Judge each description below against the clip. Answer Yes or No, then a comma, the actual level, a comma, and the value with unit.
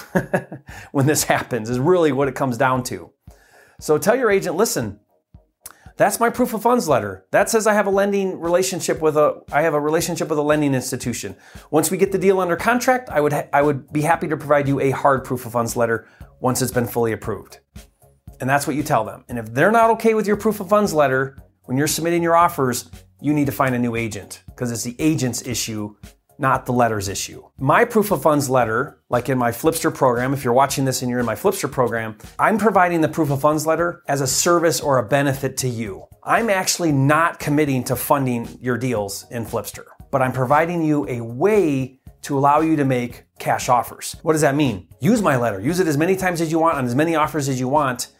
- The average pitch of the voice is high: No, medium, 140 Hz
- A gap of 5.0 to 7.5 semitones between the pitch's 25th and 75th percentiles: Yes, wide, 5.4 semitones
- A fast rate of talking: Yes, fast, 230 wpm